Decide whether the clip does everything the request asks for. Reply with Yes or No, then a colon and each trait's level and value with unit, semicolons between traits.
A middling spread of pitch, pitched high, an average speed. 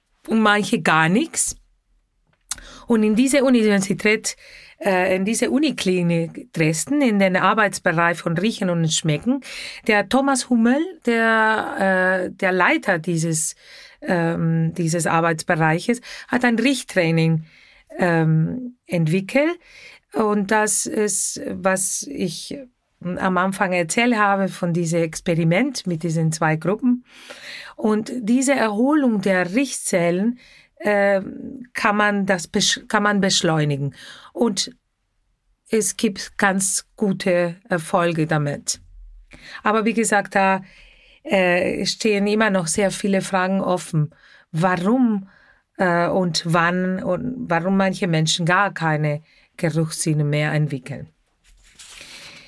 No: average, 4.8 semitones; high, 195 Hz; slow, 110 wpm